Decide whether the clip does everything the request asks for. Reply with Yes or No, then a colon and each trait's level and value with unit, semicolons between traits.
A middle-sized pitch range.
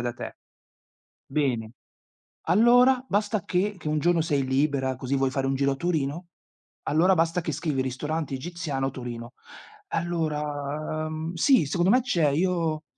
Yes: average, 4.3 semitones